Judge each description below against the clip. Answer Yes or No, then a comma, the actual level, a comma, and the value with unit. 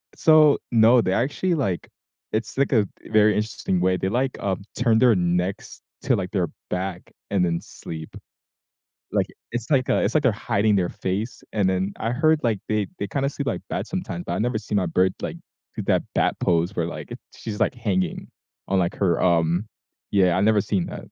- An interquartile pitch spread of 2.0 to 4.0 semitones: No, average, 4.8 semitones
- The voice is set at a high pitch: No, low, 105 Hz